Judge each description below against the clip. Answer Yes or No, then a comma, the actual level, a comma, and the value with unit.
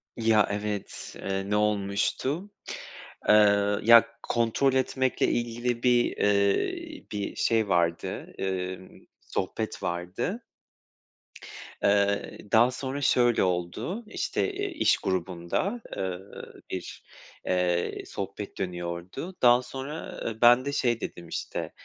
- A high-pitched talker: No, low, 105 Hz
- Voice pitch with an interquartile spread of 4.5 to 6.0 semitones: Yes, average, 5.1 semitones